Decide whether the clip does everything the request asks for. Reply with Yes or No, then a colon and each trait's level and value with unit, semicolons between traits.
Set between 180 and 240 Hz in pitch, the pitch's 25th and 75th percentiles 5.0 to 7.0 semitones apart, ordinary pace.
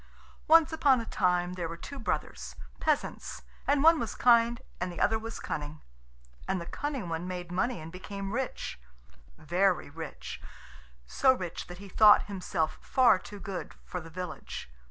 Yes: high, 190 Hz; average, 5.3 semitones; average, 165 wpm